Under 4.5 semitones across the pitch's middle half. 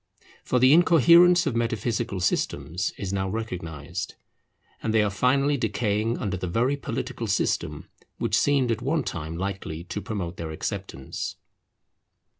No: wide, 5.6 semitones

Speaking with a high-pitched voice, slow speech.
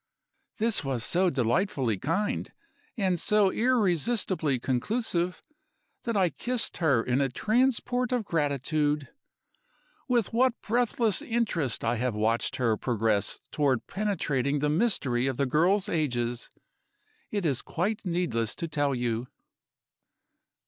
No: medium, 160 Hz; slow, 120 wpm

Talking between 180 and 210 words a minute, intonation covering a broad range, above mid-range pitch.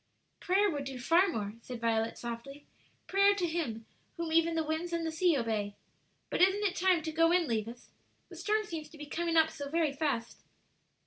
Yes: average, 200 wpm; wide, 5.8 semitones; very high, 320 Hz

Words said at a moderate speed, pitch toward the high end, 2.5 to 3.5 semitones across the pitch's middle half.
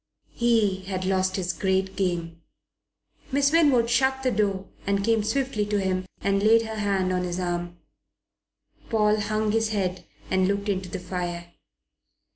Yes: average, 155 wpm; high, 195 Hz; average, 2.9 semitones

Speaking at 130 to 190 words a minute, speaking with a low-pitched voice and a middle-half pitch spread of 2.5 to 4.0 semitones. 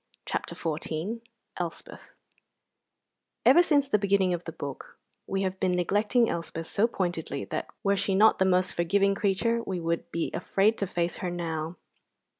No: average, 160 wpm; high, 190 Hz; average, 3.1 semitones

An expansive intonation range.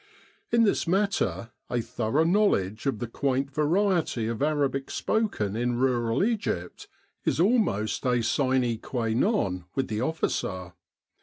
Yes: wide, 7.2 semitones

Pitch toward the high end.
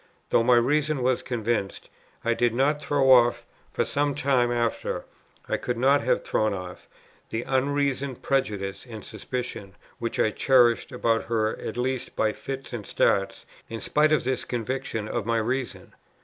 No: low, 120 Hz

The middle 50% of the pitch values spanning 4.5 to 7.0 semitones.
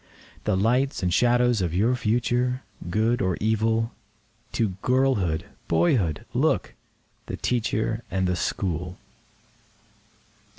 Yes: average, 4.9 semitones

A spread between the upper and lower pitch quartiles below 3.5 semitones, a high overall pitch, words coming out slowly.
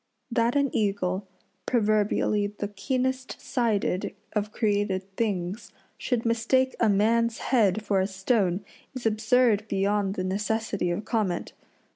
Yes: average, 2.9 semitones; high, 210 Hz; slow, 125 wpm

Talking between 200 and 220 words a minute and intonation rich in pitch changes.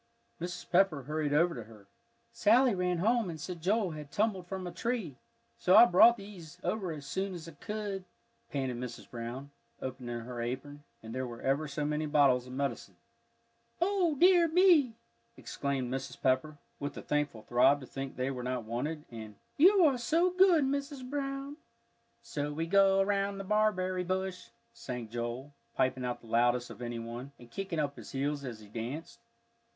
No: average, 175 wpm; wide, 7.8 semitones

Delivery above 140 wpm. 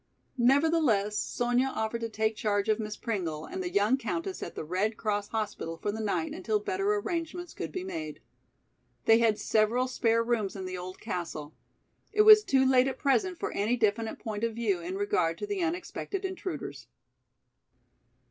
Yes: average, 175 wpm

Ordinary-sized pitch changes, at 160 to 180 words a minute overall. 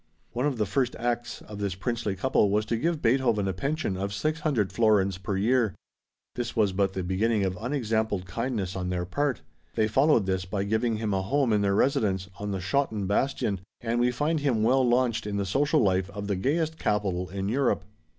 No: average, 4.4 semitones; fast, 205 wpm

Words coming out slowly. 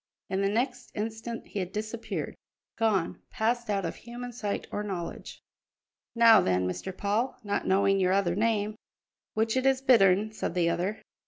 No: average, 170 wpm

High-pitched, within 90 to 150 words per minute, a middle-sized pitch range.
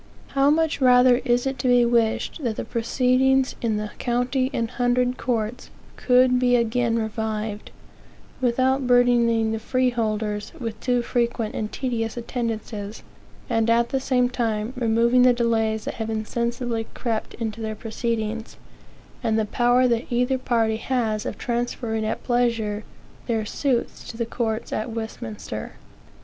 No: high, 235 Hz; average, 145 wpm; narrow, 2.0 semitones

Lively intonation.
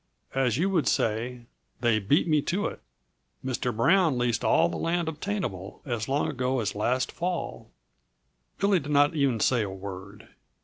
Yes: wide, 6.4 semitones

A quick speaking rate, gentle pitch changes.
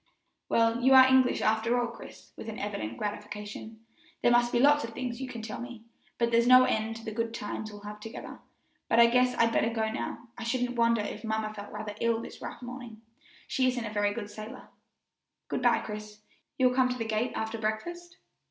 Yes: fast, 215 wpm; narrow, 2.2 semitones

